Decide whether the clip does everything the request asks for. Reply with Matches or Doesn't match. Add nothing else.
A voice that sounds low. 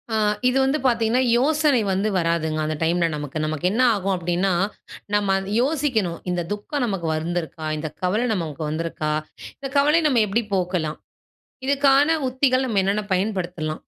Doesn't match